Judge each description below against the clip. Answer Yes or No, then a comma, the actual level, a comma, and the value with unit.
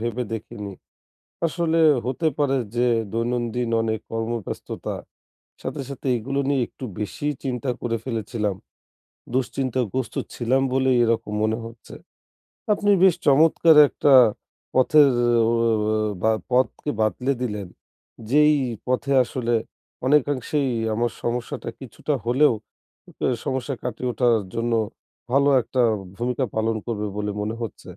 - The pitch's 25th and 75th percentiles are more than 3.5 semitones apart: No, average, 3.1 semitones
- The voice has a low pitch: Yes, low, 125 Hz